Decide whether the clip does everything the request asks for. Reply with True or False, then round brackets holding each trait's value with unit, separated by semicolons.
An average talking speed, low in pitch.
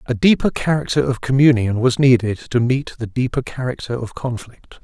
True (175 wpm; 125 Hz)